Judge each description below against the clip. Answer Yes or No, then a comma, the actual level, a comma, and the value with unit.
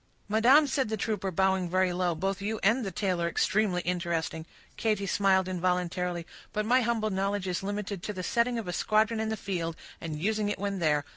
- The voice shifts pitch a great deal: No, average, 3.2 semitones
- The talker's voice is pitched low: No, high, 195 Hz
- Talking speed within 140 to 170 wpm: No, average, 195 wpm